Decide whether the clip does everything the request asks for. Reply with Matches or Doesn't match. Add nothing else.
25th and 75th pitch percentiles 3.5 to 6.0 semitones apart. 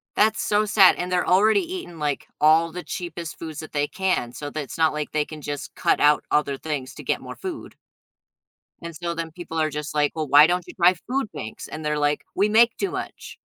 Matches